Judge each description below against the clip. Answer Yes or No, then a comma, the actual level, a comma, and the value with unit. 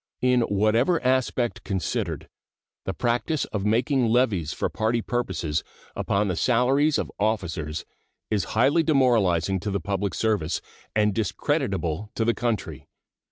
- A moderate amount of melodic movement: Yes, average, 4.2 semitones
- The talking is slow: Yes, slow, 130 wpm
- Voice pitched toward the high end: No, low, 110 Hz